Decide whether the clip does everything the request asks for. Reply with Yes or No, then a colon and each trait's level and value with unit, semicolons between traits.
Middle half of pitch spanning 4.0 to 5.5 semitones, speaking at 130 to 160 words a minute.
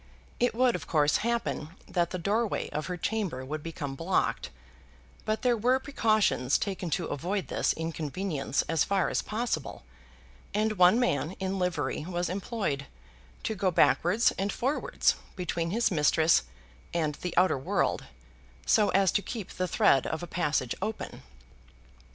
Yes: average, 5.2 semitones; average, 150 wpm